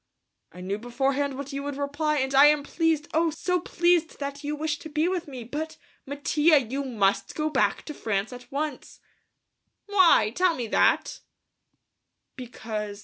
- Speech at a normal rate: Yes, average, 165 wpm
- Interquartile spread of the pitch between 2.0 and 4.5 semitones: Yes, average, 3.9 semitones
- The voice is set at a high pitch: Yes, very high, 285 Hz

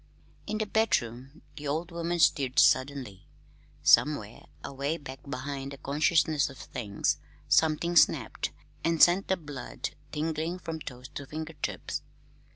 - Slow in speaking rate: Yes, slow, 130 wpm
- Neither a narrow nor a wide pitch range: Yes, average, 3.6 semitones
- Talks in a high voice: No, medium, 150 Hz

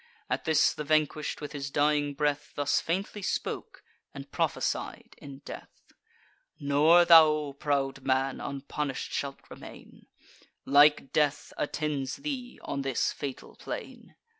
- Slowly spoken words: Yes, slow, 125 wpm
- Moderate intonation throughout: No, narrow, 1.7 semitones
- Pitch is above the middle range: No, medium, 145 Hz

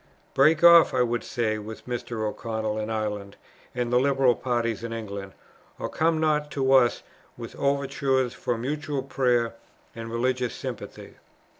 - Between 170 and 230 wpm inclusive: No, average, 150 wpm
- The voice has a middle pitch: No, low, 125 Hz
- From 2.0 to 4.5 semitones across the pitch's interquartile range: Yes, average, 3.3 semitones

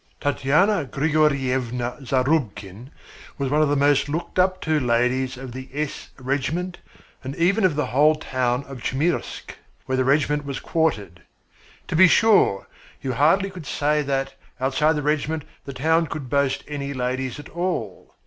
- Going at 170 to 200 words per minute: No, average, 160 wpm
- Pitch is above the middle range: No, medium, 140 Hz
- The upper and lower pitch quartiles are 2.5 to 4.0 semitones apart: Yes, average, 3.1 semitones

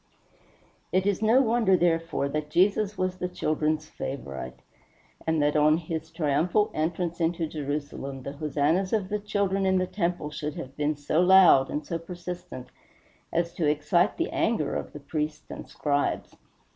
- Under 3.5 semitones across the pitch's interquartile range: No, average, 3.8 semitones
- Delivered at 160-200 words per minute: Yes, average, 165 wpm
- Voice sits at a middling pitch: Yes, medium, 165 Hz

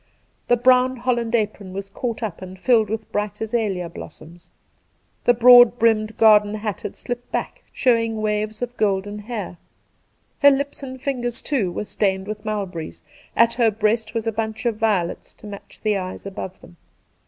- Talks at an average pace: Yes, average, 170 wpm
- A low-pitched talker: No, high, 215 Hz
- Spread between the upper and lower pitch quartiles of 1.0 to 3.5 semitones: Yes, average, 2.9 semitones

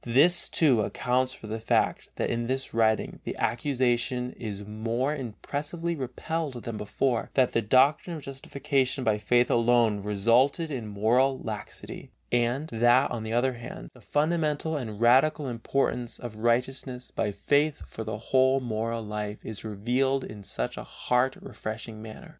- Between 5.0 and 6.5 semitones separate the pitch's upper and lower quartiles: No, average, 3.4 semitones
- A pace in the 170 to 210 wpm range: No, average, 155 wpm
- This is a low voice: Yes, low, 120 Hz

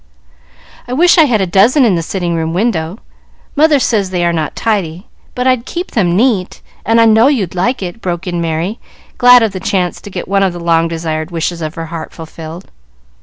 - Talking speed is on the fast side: Yes, fast, 215 wpm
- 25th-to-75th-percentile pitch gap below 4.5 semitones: No, average, 5.3 semitones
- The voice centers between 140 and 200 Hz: Yes, medium, 185 Hz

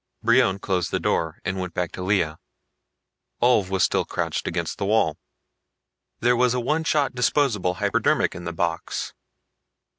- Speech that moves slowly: No, average, 155 wpm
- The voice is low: Yes, low, 100 Hz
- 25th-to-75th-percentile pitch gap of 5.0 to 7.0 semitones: Yes, wide, 5.4 semitones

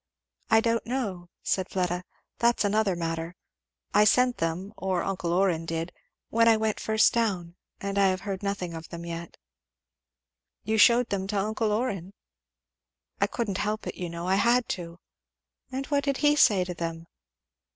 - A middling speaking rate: Yes, average, 165 wpm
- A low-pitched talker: No, high, 195 Hz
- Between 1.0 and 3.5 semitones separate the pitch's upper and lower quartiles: No, average, 4.1 semitones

